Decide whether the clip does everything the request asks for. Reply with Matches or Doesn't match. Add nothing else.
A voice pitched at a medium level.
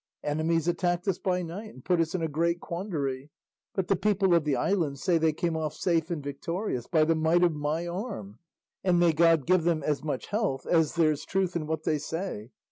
Matches